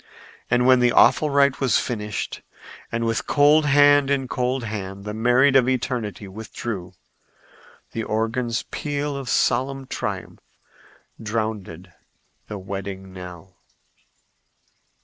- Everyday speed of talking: No, slow, 115 wpm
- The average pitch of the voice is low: Yes, low, 115 Hz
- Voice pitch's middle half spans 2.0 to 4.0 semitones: No, average, 4.5 semitones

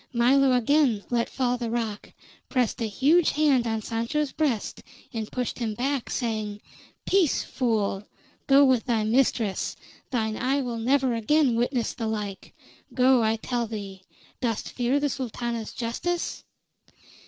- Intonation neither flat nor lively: Yes, average, 3.2 semitones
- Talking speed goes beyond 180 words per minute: No, average, 140 wpm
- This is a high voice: Yes, high, 240 Hz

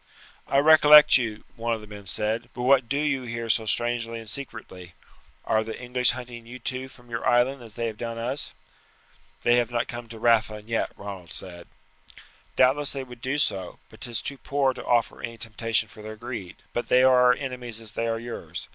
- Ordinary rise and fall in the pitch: No, narrow, 2.3 semitones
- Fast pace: Yes, fast, 210 wpm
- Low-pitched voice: Yes, low, 120 Hz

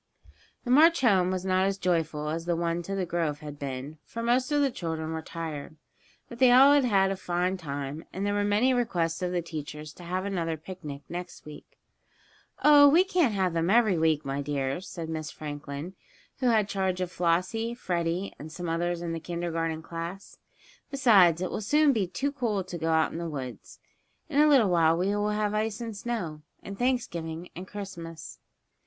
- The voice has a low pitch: No, medium, 180 Hz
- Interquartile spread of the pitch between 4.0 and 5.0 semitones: Yes, average, 4.6 semitones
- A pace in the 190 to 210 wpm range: Yes, average, 200 wpm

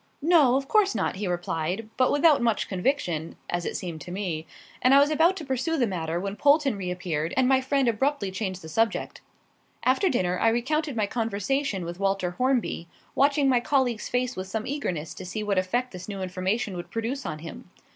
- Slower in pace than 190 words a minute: No, average, 200 wpm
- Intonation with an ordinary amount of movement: No, wide, 6.7 semitones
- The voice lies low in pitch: No, high, 225 Hz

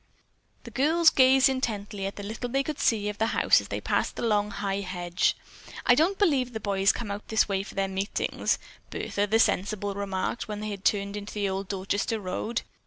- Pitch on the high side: Yes, high, 205 Hz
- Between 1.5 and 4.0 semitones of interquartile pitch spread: Yes, average, 3.3 semitones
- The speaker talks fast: Yes, fast, 210 wpm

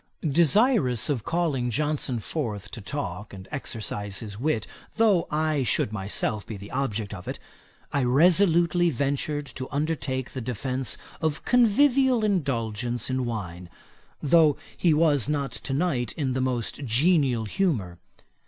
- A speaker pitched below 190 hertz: Yes, low, 135 Hz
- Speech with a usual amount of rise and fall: No, wide, 5.9 semitones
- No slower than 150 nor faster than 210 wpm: No, average, 140 wpm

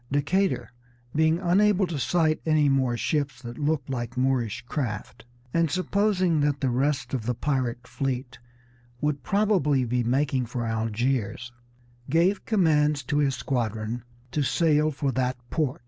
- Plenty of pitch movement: No, average, 4.2 semitones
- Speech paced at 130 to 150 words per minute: Yes, average, 145 wpm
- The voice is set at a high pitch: No, medium, 140 Hz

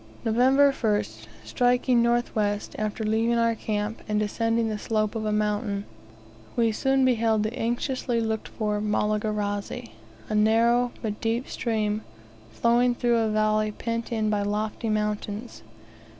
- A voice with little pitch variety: Yes, narrow, 1.8 semitones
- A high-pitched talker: Yes, high, 220 Hz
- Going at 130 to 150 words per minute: Yes, average, 140 wpm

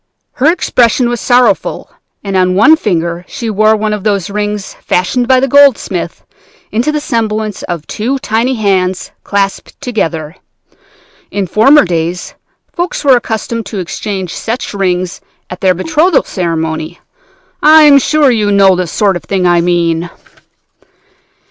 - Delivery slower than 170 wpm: Yes, average, 145 wpm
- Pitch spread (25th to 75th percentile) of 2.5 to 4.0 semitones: No, average, 5.2 semitones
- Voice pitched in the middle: No, high, 205 Hz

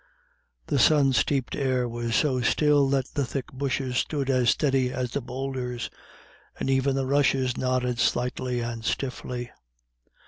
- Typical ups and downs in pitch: No, narrow, 1.7 semitones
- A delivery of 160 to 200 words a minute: No, average, 145 wpm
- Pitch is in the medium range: No, low, 130 Hz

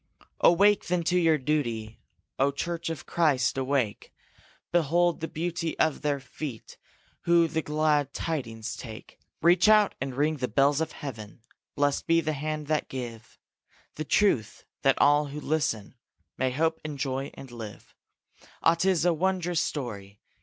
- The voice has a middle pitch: Yes, medium, 150 Hz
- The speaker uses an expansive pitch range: No, average, 4.0 semitones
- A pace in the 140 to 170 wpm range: Yes, average, 155 wpm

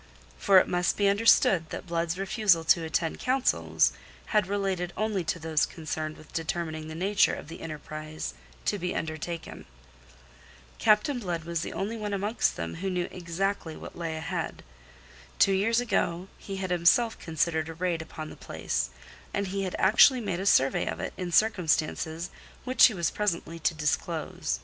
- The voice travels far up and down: No, average, 3.7 semitones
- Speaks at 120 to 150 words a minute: No, average, 170 wpm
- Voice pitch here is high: No, medium, 175 Hz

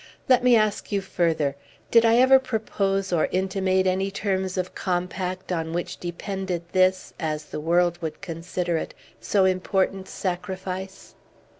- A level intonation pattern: Yes, narrow, 1.8 semitones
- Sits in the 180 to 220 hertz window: Yes, medium, 185 Hz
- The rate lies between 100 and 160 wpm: Yes, average, 145 wpm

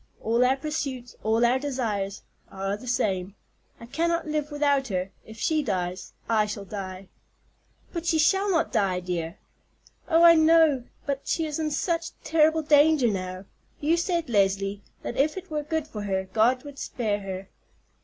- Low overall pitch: No, very high, 250 Hz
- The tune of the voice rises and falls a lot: Yes, wide, 7.7 semitones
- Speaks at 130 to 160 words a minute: No, average, 170 wpm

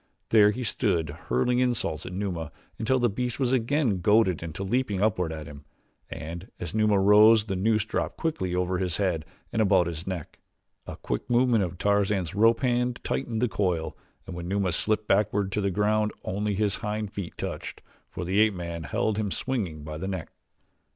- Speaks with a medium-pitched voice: No, low, 100 Hz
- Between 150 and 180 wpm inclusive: No, average, 190 wpm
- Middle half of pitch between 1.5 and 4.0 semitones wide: Yes, average, 3.6 semitones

